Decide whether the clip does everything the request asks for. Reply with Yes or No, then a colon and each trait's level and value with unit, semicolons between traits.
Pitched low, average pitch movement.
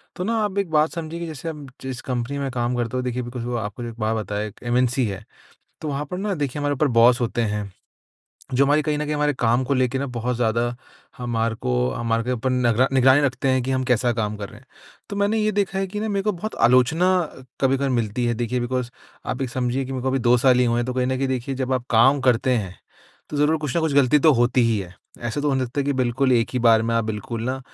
Yes: low, 125 Hz; average, 3.2 semitones